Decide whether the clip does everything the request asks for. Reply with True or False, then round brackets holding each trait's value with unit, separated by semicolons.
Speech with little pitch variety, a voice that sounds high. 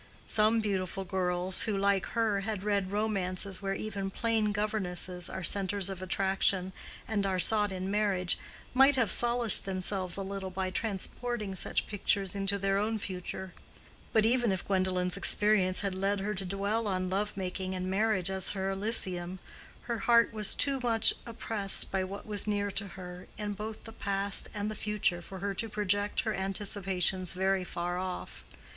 True (2.1 semitones; 195 Hz)